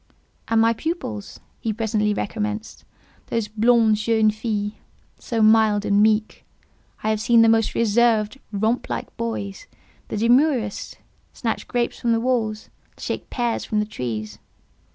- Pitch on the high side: Yes, high, 220 Hz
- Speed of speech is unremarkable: No, slow, 125 wpm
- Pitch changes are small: Yes, narrow, 1.7 semitones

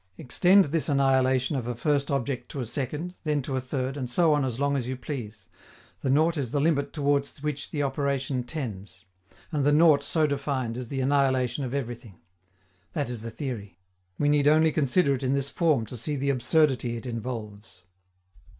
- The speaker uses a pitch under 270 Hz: Yes, low, 135 Hz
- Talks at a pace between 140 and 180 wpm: No, average, 195 wpm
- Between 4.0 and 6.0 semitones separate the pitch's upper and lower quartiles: No, average, 2.9 semitones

